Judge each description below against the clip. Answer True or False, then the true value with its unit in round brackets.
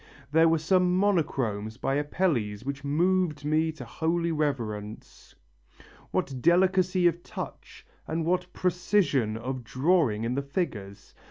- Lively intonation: True (5.9 semitones)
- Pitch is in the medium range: True (155 Hz)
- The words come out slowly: True (125 wpm)